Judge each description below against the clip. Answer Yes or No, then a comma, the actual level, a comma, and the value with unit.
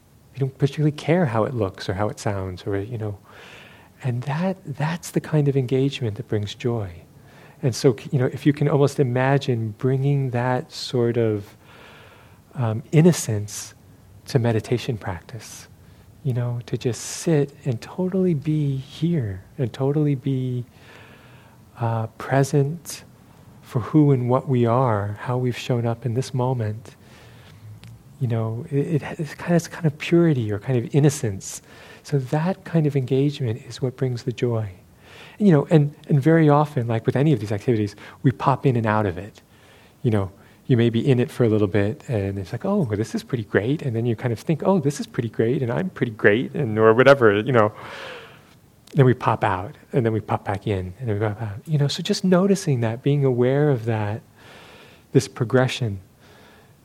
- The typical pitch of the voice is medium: No, low, 125 Hz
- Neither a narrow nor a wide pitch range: Yes, average, 4.4 semitones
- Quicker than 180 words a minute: Yes, average, 190 wpm